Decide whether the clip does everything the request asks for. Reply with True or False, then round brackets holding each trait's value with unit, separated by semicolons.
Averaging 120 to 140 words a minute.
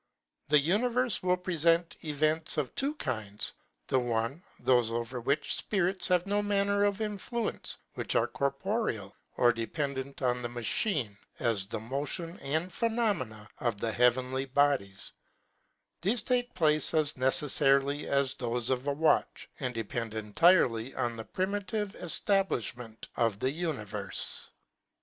True (135 wpm)